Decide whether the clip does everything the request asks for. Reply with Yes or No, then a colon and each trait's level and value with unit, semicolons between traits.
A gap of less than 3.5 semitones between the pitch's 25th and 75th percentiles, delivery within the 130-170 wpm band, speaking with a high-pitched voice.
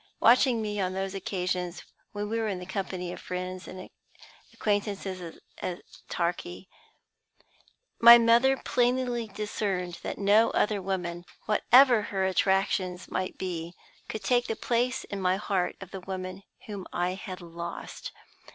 Yes: average, 3.0 semitones; average, 140 wpm; high, 195 Hz